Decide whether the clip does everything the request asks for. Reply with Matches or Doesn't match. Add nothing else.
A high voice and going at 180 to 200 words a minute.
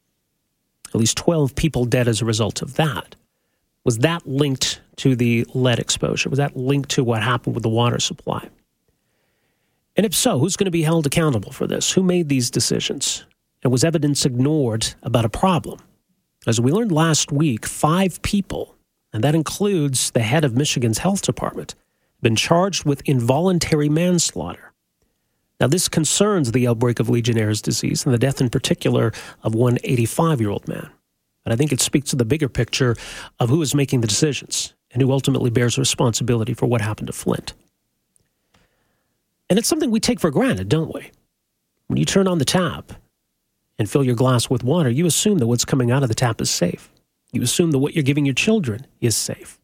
Doesn't match